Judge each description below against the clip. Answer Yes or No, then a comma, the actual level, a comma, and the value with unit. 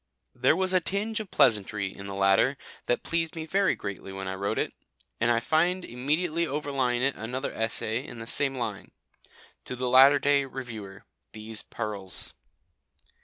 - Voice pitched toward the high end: No, low, 125 Hz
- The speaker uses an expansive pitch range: Yes, wide, 6.3 semitones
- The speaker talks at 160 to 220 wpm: Yes, average, 170 wpm